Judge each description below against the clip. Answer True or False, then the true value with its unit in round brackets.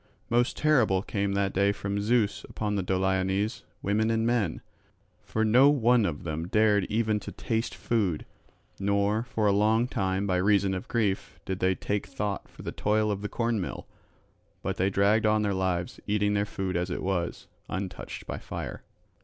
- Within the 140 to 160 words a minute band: False (180 wpm)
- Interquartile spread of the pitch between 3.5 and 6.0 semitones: False (2.4 semitones)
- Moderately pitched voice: False (100 Hz)